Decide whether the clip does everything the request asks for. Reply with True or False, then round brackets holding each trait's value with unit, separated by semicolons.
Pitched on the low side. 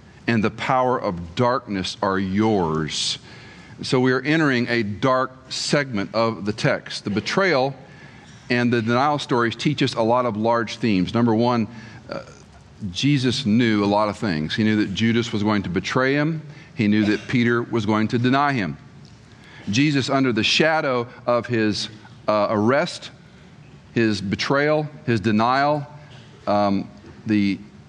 True (115 Hz)